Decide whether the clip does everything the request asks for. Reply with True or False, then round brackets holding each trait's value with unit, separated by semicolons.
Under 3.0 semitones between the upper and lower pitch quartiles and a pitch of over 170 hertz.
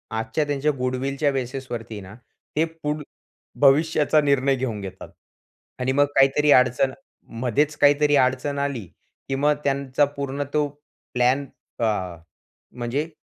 False (2.4 semitones; 135 Hz)